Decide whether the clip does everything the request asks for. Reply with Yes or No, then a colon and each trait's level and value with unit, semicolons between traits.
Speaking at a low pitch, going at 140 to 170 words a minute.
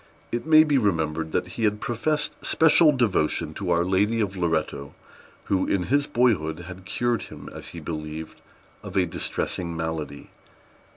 Yes: very low, 95 Hz; average, 160 wpm